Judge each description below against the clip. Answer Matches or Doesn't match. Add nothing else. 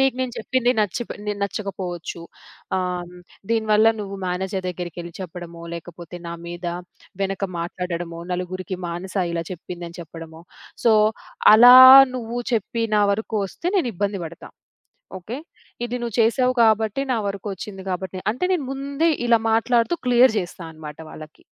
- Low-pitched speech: Doesn't match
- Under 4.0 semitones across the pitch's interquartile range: Doesn't match